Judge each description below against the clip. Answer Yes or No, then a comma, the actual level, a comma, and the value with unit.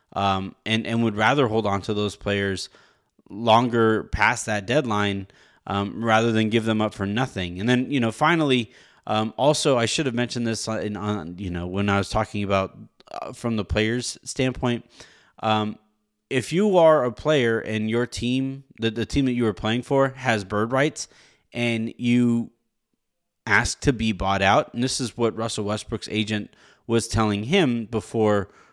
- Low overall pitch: Yes, low, 110 Hz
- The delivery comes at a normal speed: Yes, average, 180 wpm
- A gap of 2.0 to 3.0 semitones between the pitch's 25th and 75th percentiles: Yes, average, 2.7 semitones